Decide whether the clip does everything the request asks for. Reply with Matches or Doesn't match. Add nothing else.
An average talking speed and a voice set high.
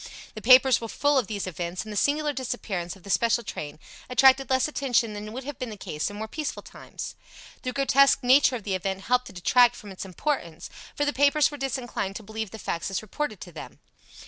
Doesn't match